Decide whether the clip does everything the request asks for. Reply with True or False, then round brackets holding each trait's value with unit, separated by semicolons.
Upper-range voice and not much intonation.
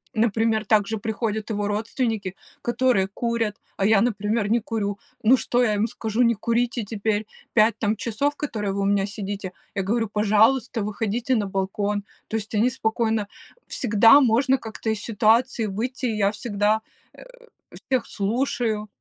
True (220 Hz; 2.2 semitones)